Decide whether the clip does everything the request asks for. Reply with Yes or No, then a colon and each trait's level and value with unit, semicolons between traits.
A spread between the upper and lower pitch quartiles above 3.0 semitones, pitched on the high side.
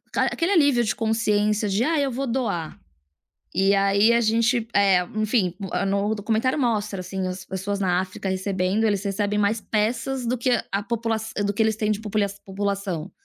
No: average, 2.7 semitones; high, 210 Hz